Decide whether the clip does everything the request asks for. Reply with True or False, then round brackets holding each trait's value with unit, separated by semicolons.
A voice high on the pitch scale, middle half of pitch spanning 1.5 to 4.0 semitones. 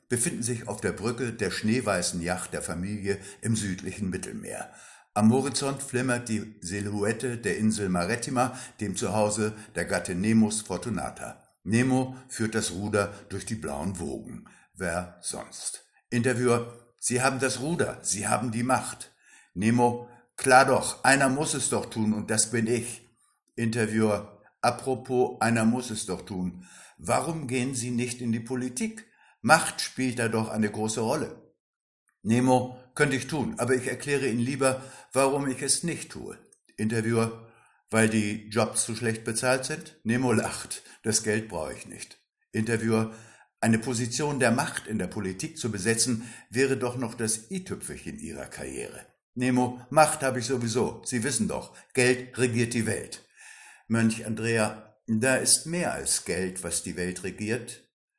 False (115 Hz; 3.0 semitones)